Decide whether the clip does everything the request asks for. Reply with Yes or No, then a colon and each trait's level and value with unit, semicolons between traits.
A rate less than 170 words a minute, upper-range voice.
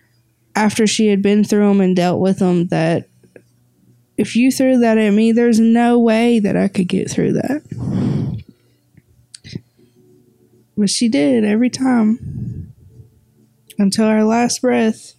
Yes: average, 140 wpm; high, 205 Hz